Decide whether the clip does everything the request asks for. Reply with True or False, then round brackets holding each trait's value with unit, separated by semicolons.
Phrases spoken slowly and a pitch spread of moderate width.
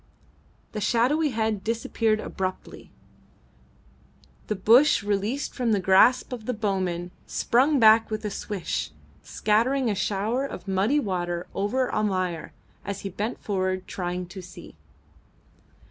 True (130 wpm; 3.7 semitones)